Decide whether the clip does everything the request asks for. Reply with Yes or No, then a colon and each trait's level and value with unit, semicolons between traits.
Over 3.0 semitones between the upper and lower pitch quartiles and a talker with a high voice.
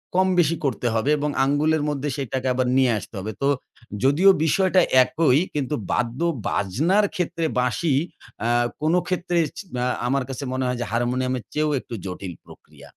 No: average, 4.6 semitones; medium, 140 Hz